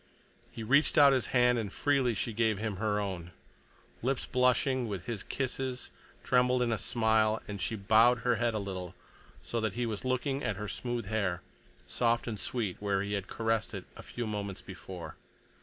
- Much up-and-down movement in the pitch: No, average, 3.4 semitones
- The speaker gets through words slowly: No, average, 190 wpm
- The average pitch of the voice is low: Yes, low, 110 Hz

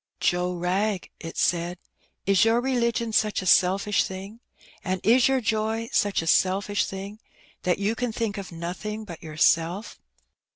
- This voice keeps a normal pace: Yes, average, 155 wpm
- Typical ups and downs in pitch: Yes, average, 3.5 semitones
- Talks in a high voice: Yes, high, 200 Hz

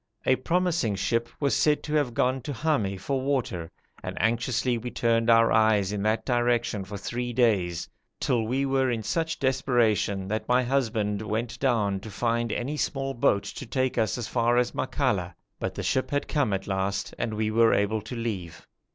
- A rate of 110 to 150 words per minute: No, average, 190 wpm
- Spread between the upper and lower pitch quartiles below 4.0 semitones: Yes, average, 3.5 semitones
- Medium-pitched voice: No, low, 115 Hz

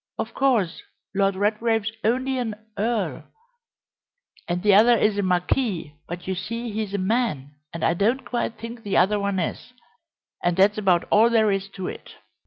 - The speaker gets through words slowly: No, average, 175 wpm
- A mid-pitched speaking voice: No, high, 210 Hz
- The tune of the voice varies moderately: Yes, average, 3.5 semitones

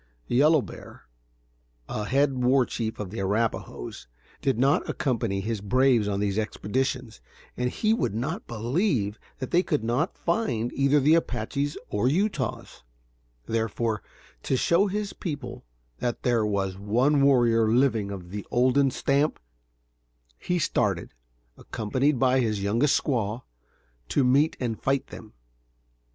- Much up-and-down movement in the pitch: No, average, 4.3 semitones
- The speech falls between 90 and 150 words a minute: Yes, average, 140 wpm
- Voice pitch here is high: No, low, 125 Hz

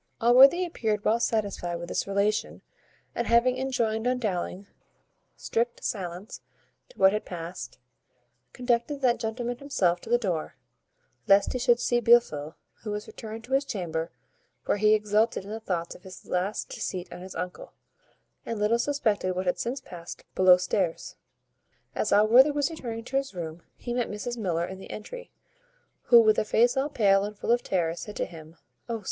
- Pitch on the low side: No, high, 215 Hz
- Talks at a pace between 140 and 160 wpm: No, average, 180 wpm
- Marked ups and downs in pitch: No, average, 4.6 semitones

